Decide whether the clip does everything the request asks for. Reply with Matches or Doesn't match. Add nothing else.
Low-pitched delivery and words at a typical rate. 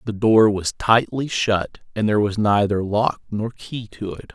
Matches